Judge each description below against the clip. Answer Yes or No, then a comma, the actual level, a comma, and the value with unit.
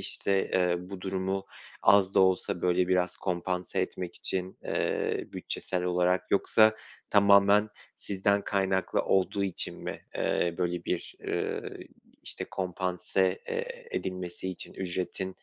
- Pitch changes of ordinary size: No, narrow, 1.5 semitones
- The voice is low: Yes, very low, 95 Hz